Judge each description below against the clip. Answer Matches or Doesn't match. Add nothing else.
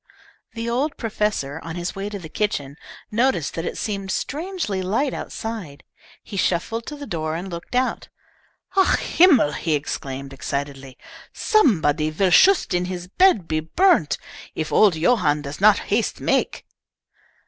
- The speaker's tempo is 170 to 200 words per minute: Doesn't match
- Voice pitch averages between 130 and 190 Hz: Matches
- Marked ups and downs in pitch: Matches